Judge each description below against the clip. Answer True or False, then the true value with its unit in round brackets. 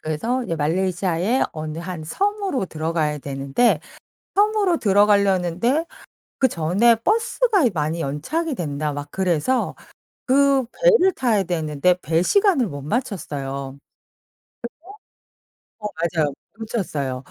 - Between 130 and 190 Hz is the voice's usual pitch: True (185 Hz)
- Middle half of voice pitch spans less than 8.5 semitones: False (8.9 semitones)